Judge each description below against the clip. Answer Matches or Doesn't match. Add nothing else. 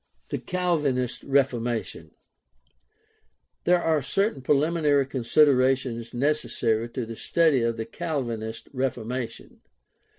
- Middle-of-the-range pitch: Doesn't match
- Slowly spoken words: Matches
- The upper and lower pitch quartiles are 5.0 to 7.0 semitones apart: Doesn't match